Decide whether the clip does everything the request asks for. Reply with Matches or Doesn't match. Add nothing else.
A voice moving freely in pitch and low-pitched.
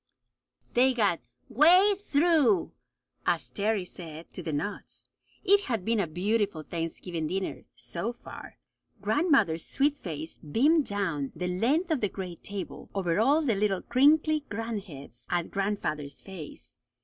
Doesn't match